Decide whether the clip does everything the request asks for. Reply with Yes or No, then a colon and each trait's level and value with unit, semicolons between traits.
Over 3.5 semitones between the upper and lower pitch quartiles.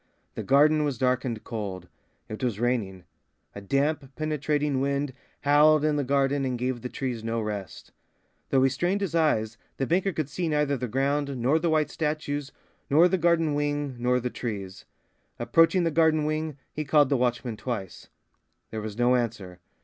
Yes: average, 4.0 semitones